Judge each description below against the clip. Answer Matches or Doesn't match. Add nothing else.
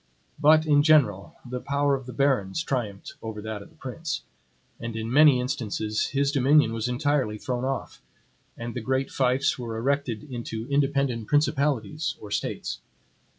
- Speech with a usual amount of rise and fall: Matches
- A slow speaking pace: Doesn't match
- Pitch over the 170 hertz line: Doesn't match